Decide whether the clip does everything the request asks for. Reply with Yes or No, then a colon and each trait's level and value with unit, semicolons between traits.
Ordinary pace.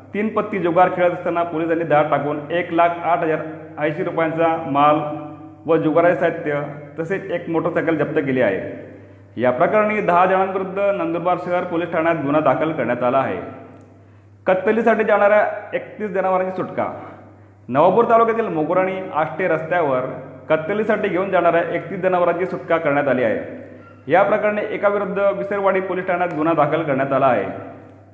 No: fast, 145 wpm